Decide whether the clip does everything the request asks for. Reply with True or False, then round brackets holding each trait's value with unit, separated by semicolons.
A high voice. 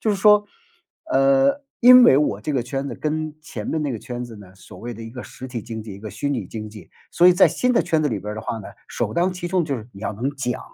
False (135 Hz)